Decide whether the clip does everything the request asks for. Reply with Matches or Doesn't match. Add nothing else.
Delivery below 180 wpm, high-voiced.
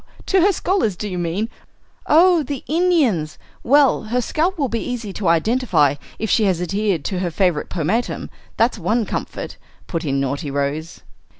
Matches